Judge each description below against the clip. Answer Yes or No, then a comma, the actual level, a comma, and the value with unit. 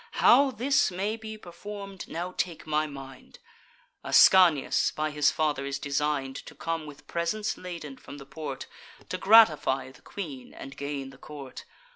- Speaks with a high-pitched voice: No, medium, 155 Hz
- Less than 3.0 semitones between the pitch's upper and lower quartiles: No, wide, 5.4 semitones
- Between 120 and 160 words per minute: Yes, average, 155 wpm